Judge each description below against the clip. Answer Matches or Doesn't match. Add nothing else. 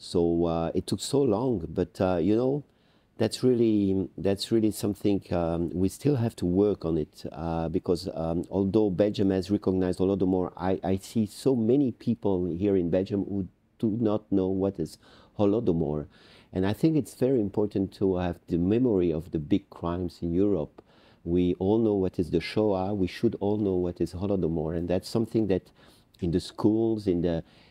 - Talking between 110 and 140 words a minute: Doesn't match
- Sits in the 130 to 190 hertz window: Doesn't match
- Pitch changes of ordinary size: Matches